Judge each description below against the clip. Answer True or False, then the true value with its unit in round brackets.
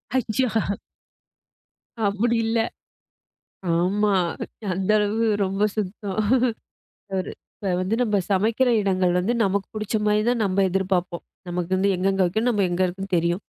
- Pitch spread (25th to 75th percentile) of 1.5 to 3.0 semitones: True (2.4 semitones)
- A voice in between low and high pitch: False (195 Hz)